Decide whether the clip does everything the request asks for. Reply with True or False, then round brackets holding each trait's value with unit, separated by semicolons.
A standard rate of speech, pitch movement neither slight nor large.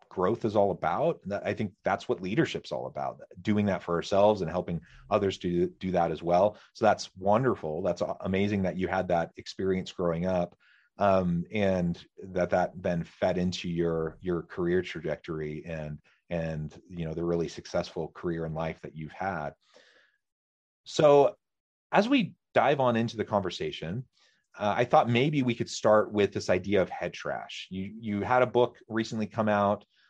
True (175 wpm; 4.0 semitones)